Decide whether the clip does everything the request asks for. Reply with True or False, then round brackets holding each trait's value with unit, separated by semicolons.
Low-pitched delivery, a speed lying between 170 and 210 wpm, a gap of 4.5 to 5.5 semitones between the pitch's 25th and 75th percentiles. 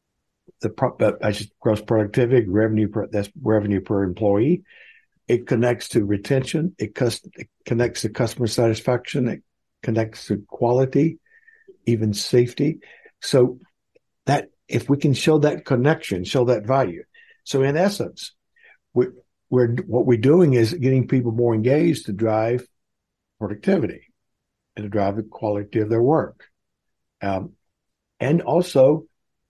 False (120 Hz; 140 wpm; 5.0 semitones)